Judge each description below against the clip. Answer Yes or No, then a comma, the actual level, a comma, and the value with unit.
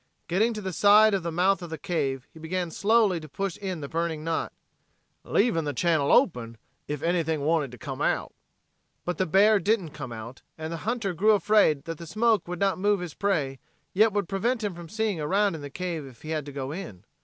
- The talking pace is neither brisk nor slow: No, fast, 220 wpm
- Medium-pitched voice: Yes, medium, 170 Hz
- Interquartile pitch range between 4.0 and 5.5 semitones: Yes, average, 4.6 semitones